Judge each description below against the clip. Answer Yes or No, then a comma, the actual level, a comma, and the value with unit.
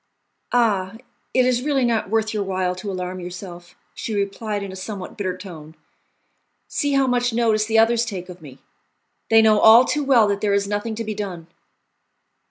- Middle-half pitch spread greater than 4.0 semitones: No, average, 3.6 semitones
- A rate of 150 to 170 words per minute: No, average, 180 wpm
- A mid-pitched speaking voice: No, high, 210 Hz